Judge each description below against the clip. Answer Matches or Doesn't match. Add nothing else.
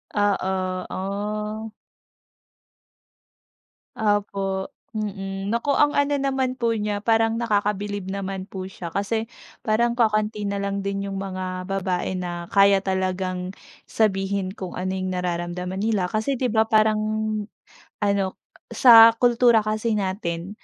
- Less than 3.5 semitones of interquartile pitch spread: Matches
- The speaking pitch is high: Matches